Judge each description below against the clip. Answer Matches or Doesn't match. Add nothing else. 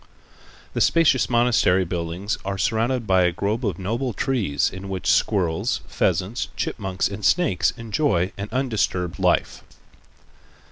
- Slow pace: Matches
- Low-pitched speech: Matches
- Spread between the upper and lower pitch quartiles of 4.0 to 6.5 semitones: Matches